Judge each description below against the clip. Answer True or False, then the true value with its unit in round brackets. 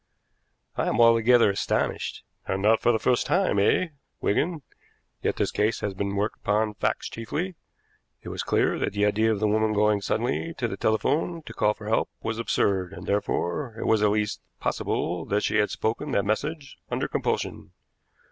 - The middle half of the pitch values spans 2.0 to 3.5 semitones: True (2.7 semitones)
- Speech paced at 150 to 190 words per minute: True (185 wpm)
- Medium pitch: False (110 Hz)